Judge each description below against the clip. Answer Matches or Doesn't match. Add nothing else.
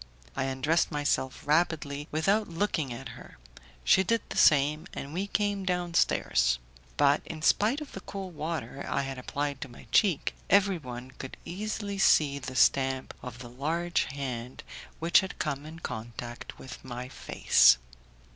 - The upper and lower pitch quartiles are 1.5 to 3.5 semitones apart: Doesn't match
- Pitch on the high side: Doesn't match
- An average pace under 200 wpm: Matches